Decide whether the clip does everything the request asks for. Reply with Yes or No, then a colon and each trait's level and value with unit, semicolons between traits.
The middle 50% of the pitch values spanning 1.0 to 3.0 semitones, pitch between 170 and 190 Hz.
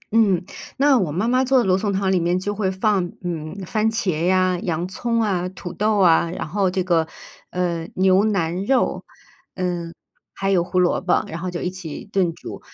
Yes: narrow, 2.6 semitones; medium, 185 Hz